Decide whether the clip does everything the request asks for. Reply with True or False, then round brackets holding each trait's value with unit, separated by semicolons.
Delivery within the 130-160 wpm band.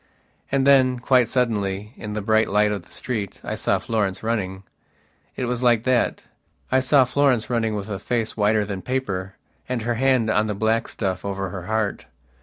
False (185 wpm)